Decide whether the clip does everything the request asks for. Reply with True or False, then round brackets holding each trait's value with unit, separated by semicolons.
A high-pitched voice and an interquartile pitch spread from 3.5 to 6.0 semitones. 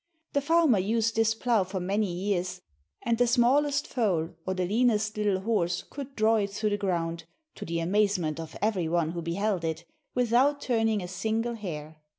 True (205 Hz; 4.5 semitones)